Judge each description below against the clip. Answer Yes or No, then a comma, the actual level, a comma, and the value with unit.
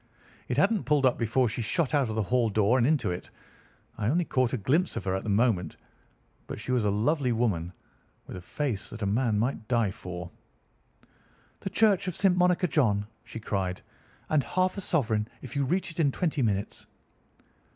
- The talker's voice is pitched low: Yes, low, 120 Hz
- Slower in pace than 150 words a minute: No, average, 200 wpm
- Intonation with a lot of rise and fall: Yes, wide, 6.3 semitones